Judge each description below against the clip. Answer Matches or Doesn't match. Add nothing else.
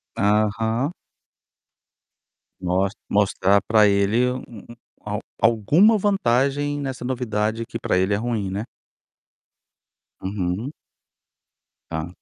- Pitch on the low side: Matches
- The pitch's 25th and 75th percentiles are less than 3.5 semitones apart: Doesn't match